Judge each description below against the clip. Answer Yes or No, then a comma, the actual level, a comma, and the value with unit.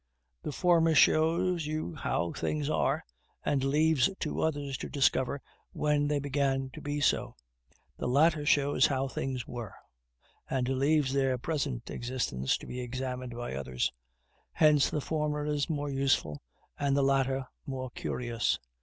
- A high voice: No, medium, 140 Hz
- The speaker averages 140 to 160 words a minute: Yes, average, 145 wpm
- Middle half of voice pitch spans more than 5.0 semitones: No, narrow, 2.5 semitones